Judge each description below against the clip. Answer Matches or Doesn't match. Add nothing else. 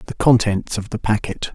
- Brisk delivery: Doesn't match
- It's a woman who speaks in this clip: Doesn't match